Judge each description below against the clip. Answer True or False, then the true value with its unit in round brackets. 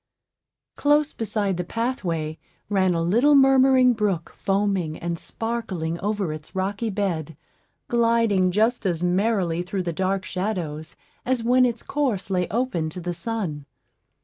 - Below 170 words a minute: True (140 wpm)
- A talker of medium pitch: False (195 Hz)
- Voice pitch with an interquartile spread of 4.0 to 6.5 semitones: True (5.0 semitones)